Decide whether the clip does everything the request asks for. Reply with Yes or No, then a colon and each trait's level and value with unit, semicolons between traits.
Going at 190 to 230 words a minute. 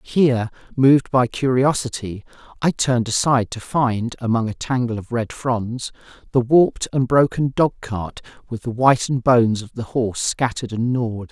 No: average, 165 wpm